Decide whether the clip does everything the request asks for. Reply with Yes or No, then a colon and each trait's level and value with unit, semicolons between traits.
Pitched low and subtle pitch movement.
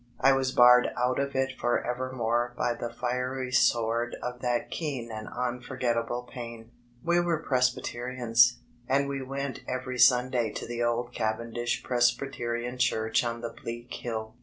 Yes: low, 120 Hz; narrow, 1.4 semitones